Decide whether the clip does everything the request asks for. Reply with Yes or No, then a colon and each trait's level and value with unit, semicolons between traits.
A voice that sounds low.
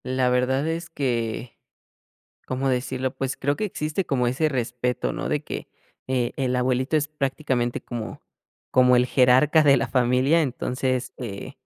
Yes: low, 130 Hz